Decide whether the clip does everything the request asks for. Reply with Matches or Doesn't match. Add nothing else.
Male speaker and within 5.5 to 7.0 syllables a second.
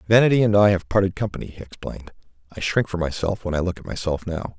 Matches